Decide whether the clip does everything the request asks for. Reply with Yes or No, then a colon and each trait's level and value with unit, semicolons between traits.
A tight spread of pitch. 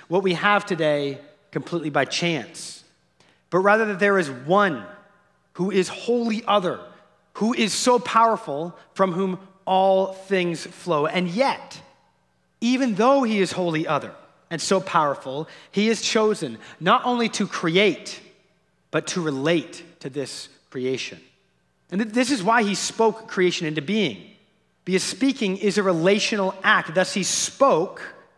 No: average, 3.9 semitones